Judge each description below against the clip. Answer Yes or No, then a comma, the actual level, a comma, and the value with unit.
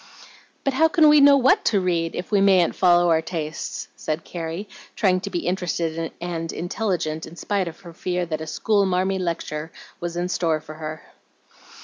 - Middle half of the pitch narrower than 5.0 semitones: Yes, average, 2.9 semitones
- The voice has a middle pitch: Yes, medium, 175 Hz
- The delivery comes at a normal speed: Yes, average, 190 wpm